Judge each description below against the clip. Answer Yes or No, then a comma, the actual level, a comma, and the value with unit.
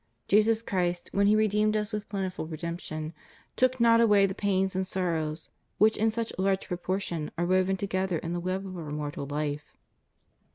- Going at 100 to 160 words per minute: No, average, 175 wpm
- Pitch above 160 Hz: Yes, high, 190 Hz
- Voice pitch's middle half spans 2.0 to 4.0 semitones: Yes, average, 3.6 semitones